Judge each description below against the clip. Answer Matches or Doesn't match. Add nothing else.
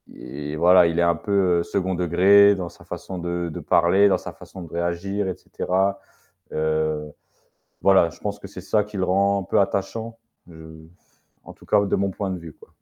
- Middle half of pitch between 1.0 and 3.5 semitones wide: Matches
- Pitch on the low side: Matches